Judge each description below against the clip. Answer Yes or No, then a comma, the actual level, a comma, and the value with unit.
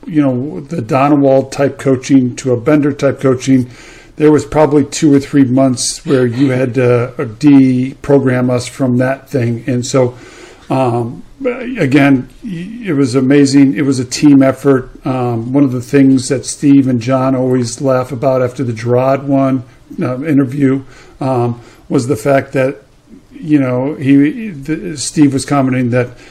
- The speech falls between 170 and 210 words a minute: No, average, 160 wpm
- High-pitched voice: No, low, 135 Hz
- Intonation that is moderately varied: No, narrow, 2.0 semitones